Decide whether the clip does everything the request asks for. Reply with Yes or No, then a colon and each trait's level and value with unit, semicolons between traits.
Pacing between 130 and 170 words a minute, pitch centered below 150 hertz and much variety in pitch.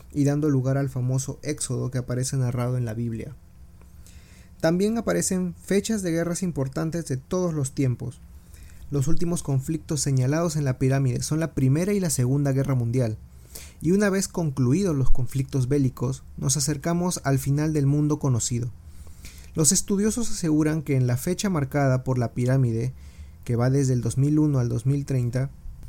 No: average, 160 wpm; low, 135 Hz; average, 4.3 semitones